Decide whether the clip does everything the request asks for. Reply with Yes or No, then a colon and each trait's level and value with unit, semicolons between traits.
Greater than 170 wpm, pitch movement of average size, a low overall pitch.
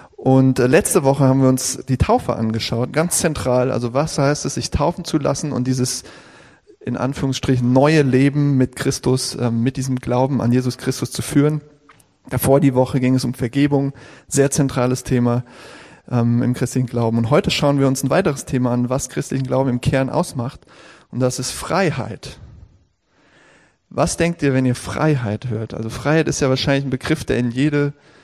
No: average, 180 wpm; narrow, 2.2 semitones; low, 130 Hz